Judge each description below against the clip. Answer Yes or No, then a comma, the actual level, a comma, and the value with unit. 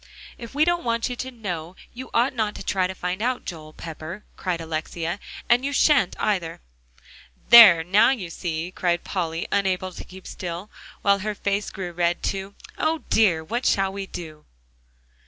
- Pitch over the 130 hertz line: Yes, high, 190 Hz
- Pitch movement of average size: Yes, average, 4.7 semitones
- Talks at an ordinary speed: Yes, average, 175 wpm